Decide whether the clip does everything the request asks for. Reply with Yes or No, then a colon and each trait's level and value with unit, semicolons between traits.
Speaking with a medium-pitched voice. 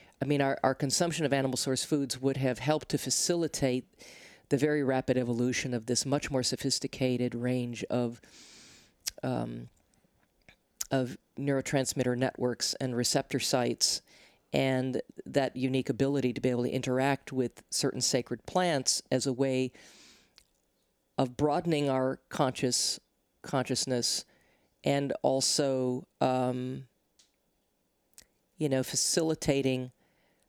No: low, 130 Hz